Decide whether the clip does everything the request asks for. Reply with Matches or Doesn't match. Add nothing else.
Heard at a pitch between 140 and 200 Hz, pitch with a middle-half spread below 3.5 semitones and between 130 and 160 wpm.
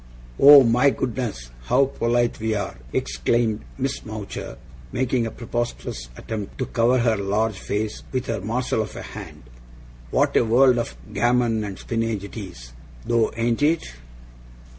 Doesn't match